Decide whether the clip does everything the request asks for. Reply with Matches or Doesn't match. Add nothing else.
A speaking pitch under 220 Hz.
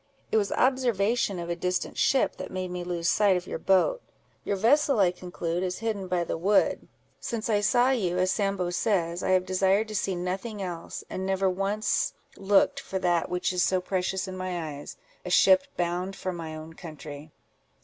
Matches